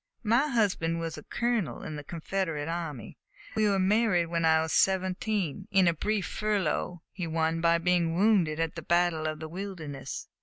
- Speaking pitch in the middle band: Yes, medium, 175 Hz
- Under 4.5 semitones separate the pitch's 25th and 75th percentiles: Yes, average, 3.5 semitones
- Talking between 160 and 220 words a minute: Yes, average, 180 wpm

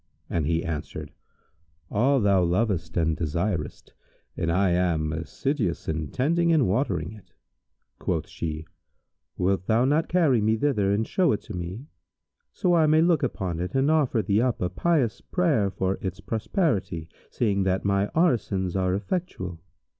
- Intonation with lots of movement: Yes, wide, 7.4 semitones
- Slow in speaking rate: No, average, 155 wpm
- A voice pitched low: Yes, low, 100 Hz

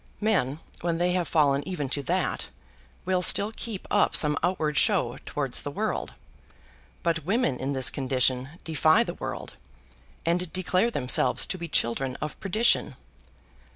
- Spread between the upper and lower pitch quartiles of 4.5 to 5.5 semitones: Yes, average, 5.0 semitones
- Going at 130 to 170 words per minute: Yes, average, 150 wpm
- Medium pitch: Yes, medium, 165 Hz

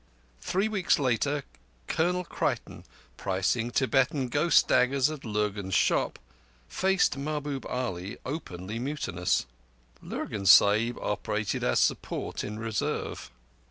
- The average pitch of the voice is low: Yes, low, 125 Hz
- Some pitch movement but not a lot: No, wide, 6.0 semitones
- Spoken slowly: Yes, slow, 105 wpm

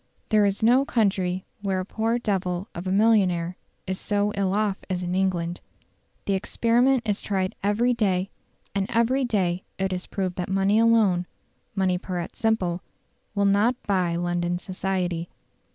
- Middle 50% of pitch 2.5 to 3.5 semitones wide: Yes, average, 2.9 semitones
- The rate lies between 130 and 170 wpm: Yes, average, 160 wpm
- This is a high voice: Yes, high, 195 Hz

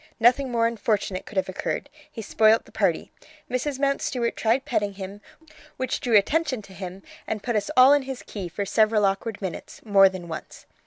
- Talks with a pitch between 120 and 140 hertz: No, high, 220 Hz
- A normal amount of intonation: Yes, average, 4.3 semitones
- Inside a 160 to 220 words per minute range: Yes, average, 190 wpm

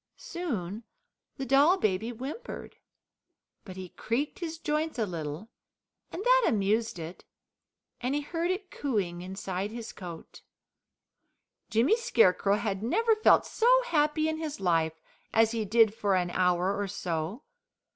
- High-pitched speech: Yes, high, 225 Hz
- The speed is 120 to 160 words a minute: Yes, average, 140 wpm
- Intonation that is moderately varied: No, wide, 8.5 semitones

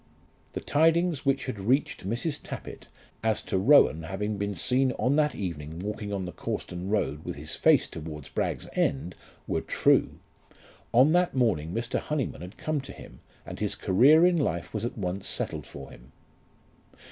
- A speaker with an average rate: Yes, average, 170 wpm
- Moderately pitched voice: No, low, 105 Hz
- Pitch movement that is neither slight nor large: No, wide, 7.6 semitones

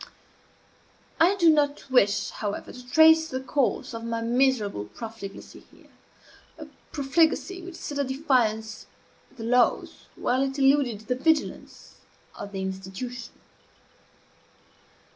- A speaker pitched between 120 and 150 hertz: No, very high, 250 Hz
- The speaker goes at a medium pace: No, slow, 120 wpm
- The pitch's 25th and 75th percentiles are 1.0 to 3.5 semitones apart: No, average, 4.7 semitones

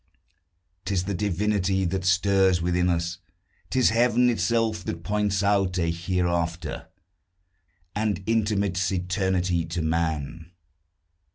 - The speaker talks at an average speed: No, slow, 105 wpm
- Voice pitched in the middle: No, very low, 95 Hz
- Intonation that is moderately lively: Yes, average, 3.0 semitones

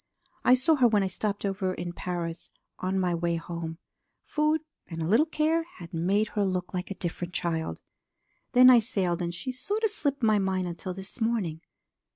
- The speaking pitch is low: No, high, 190 Hz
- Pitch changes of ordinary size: No, wide, 5.8 semitones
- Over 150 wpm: Yes, average, 195 wpm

